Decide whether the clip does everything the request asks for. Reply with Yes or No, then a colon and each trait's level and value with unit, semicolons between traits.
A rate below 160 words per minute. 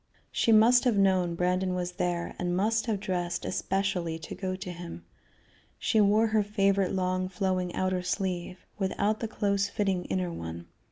No: average, 165 wpm